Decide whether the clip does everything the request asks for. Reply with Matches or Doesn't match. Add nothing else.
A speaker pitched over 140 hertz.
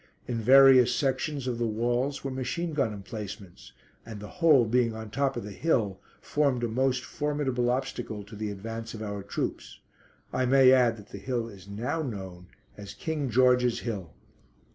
Doesn't match